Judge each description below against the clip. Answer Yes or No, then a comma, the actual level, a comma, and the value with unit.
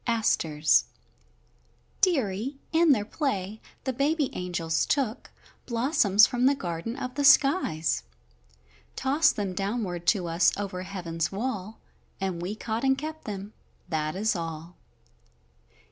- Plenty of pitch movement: Yes, wide, 6.8 semitones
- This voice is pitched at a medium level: No, high, 210 Hz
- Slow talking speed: Yes, slow, 125 wpm